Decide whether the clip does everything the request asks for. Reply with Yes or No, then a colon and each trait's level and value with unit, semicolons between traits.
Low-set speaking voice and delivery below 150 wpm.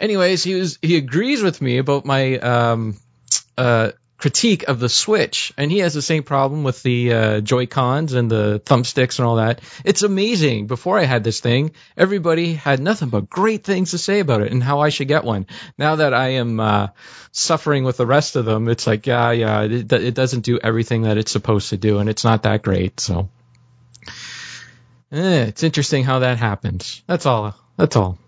No: low, 125 Hz; fast, 205 wpm